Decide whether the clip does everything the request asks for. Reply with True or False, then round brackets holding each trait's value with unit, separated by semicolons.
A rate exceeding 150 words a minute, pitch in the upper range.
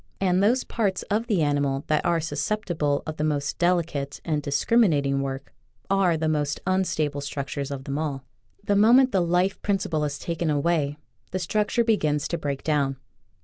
False (170 wpm; 155 Hz)